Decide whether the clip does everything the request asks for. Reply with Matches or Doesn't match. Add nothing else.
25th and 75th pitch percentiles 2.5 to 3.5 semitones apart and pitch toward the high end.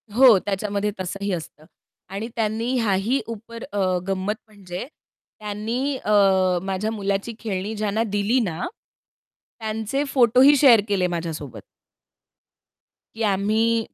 Matches